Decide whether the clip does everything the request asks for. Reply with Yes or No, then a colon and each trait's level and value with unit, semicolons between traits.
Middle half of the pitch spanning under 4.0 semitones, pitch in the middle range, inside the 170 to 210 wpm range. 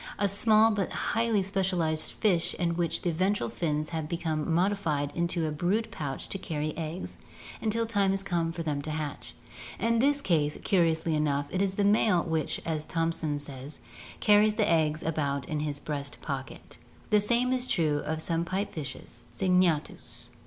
No: average, 4.5 semitones; medium, 170 Hz; average, 175 wpm